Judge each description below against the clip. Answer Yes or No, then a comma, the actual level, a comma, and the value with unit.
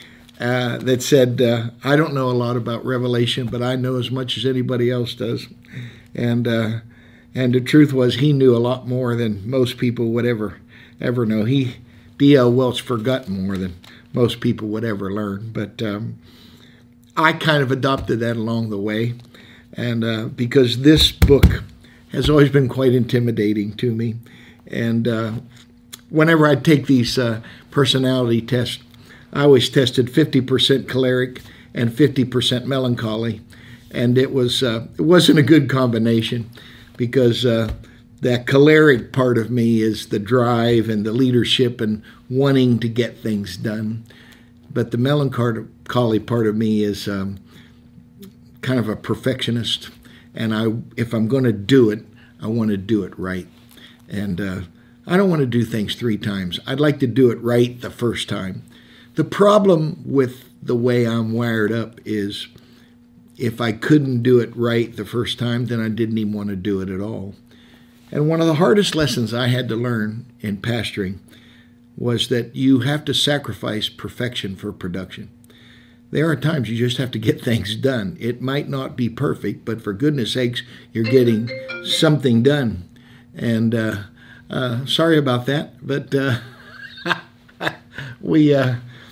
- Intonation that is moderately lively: No, narrow, 2.1 semitones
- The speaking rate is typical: Yes, average, 165 wpm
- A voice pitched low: Yes, low, 120 Hz